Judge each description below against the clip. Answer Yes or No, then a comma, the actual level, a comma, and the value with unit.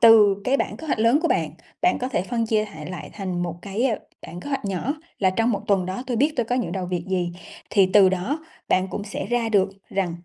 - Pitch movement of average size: Yes, average, 4.5 semitones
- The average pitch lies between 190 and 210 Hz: Yes, high, 205 Hz